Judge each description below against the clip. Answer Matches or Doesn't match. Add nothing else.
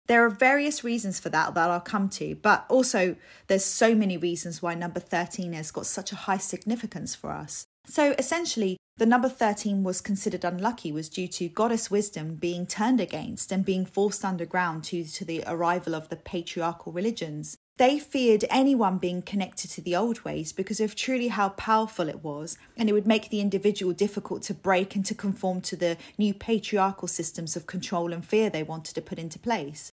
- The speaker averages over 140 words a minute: Matches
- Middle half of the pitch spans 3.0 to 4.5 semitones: Matches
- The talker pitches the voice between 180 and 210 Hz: Matches